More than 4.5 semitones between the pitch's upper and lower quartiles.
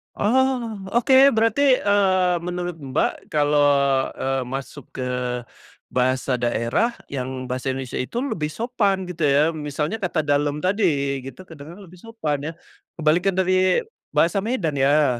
Yes: wide, 5.6 semitones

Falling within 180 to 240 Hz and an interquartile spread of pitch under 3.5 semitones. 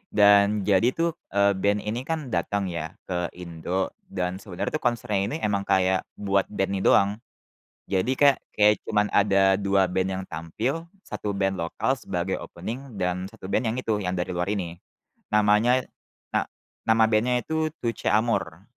No: low, 100 Hz; narrow, 2.5 semitones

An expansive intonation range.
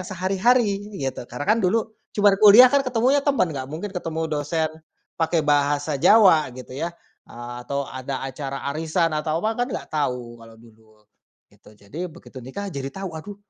Yes: wide, 6.7 semitones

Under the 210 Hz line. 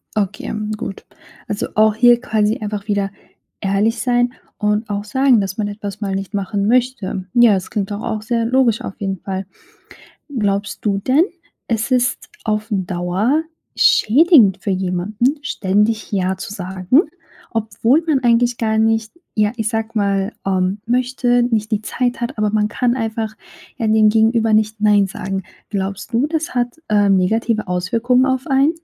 No: high, 215 Hz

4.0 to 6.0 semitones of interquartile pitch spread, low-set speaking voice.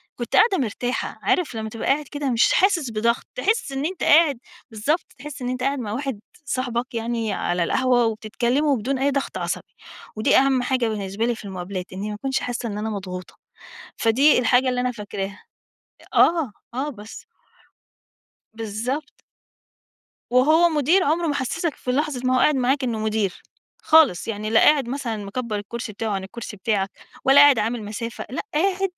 No: average, 4.6 semitones; high, 245 Hz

